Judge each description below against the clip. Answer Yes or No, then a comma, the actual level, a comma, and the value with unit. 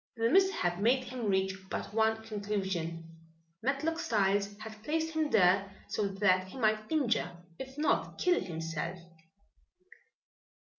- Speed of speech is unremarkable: No, slow, 130 wpm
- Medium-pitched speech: No, high, 215 Hz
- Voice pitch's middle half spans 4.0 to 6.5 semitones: Yes, average, 5.2 semitones